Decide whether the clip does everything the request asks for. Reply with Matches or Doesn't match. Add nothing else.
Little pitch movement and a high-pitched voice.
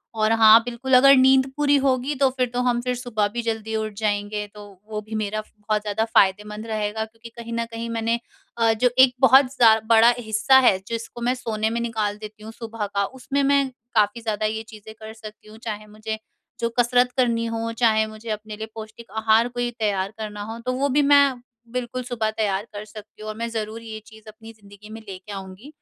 Matches